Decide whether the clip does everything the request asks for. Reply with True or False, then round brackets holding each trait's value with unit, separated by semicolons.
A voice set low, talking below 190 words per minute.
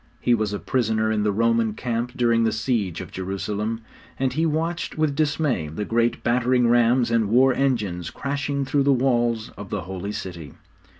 True (115 Hz; 180 wpm)